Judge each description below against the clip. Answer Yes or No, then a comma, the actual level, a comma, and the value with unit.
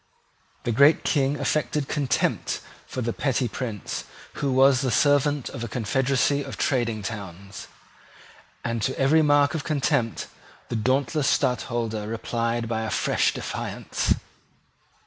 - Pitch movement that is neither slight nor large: Yes, average, 3.7 semitones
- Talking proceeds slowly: Yes, slow, 130 wpm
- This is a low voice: Yes, low, 130 Hz